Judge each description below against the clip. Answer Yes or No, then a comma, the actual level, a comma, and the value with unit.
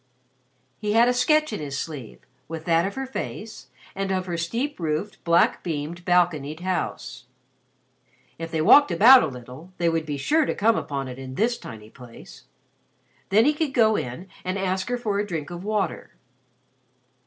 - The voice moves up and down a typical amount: No, wide, 5.9 semitones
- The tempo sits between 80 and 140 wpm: No, average, 175 wpm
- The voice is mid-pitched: Yes, medium, 180 Hz